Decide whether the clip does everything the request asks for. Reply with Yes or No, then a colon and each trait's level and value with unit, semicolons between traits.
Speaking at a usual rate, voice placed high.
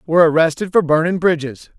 No: average, 170 wpm; medium, 165 Hz